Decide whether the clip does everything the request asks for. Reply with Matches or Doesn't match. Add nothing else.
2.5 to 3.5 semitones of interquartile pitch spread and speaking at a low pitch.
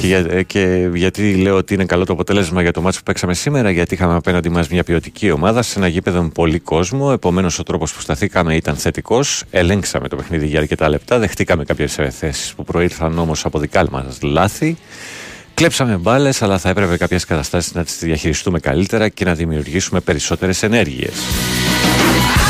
Matches